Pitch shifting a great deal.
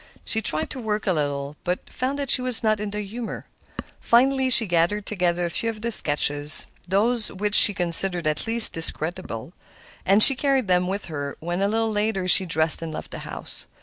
No: average, 4.9 semitones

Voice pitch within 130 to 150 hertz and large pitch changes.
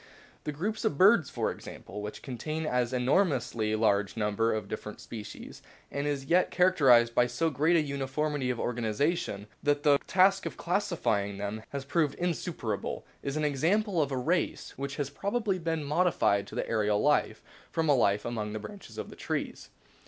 Yes: medium, 140 Hz; wide, 6.4 semitones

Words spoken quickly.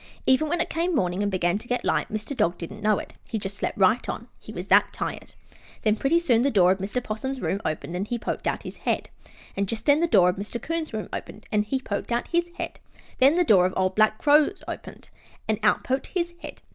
Yes: fast, 250 wpm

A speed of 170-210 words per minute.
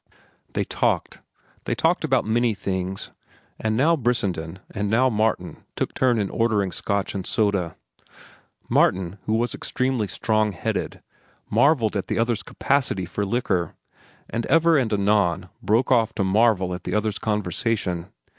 No: average, 145 wpm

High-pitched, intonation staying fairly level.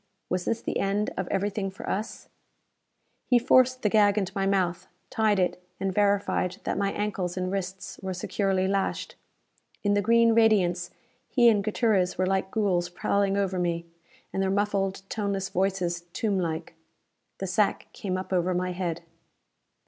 Yes: high, 195 Hz; narrow, 2.0 semitones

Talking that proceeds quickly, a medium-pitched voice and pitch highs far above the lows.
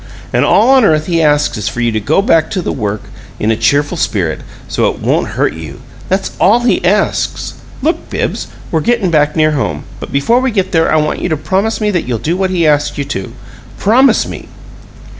Yes: fast, 220 wpm; medium, 155 Hz; wide, 5.8 semitones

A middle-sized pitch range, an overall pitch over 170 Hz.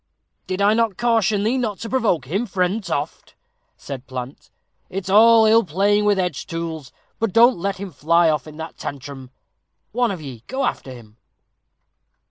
No: wide, 6.5 semitones; high, 190 Hz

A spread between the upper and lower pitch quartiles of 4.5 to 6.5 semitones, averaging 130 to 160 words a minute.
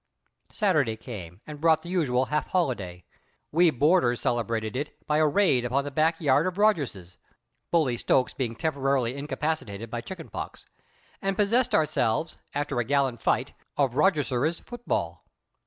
Yes: average, 5.2 semitones; average, 150 wpm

